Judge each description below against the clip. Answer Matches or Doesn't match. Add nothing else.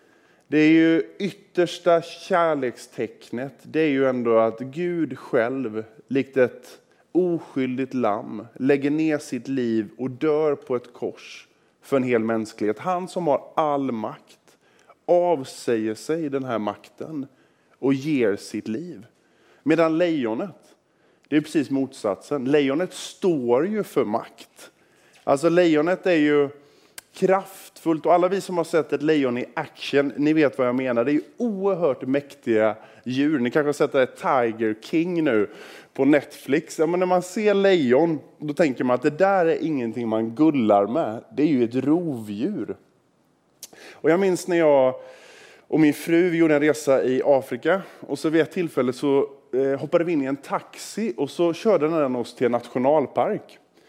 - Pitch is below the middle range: Doesn't match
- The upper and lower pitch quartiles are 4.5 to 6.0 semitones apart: Matches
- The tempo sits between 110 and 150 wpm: Doesn't match